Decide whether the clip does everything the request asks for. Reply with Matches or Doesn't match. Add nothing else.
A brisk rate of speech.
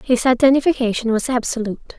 Doesn't match